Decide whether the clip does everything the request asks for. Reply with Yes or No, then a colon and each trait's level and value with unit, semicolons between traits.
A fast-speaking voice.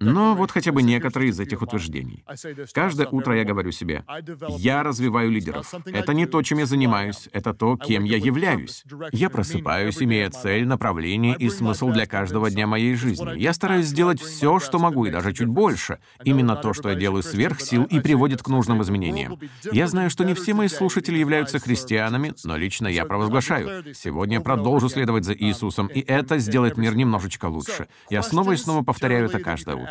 Yes: fast, 185 wpm